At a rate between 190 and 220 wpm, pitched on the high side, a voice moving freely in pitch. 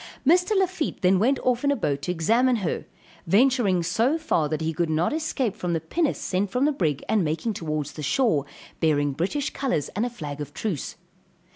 Yes: fast, 205 wpm; high, 195 Hz; wide, 8.9 semitones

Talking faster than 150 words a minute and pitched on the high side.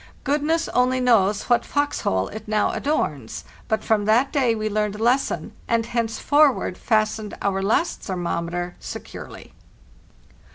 No: average, 140 wpm; high, 220 Hz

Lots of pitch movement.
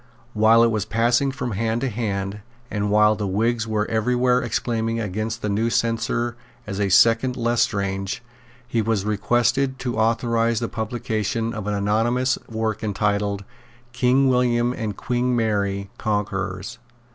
No: narrow, 2.5 semitones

